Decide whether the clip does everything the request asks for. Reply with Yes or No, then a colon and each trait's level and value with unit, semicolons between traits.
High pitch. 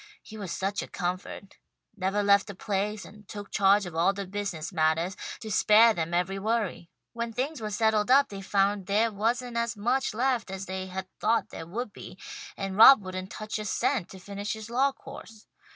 Yes: high, 205 Hz